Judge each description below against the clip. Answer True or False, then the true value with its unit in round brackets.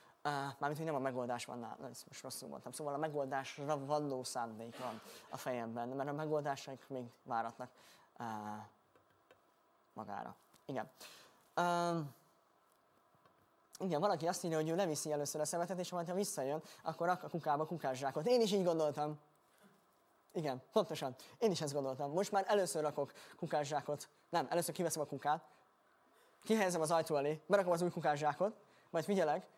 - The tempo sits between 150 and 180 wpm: True (155 wpm)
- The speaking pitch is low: False (150 Hz)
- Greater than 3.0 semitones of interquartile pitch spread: True (4.1 semitones)